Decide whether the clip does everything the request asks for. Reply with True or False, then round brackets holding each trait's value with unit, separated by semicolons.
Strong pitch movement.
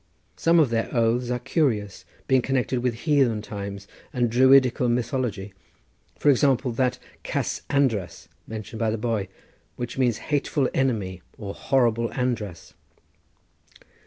False (3.2 semitones)